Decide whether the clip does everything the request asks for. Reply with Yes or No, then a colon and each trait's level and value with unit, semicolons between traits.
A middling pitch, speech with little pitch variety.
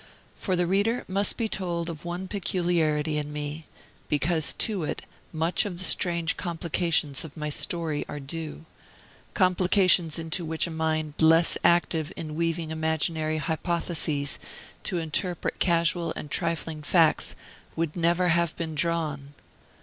Yes: medium, 165 Hz; narrow, 1.9 semitones